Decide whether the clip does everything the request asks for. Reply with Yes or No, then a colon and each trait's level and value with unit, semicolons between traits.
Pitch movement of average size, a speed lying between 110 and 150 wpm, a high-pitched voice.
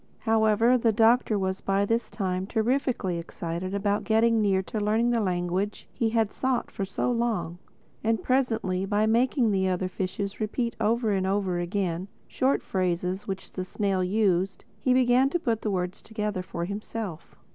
No: average, 3.4 semitones; average, 160 wpm; high, 205 Hz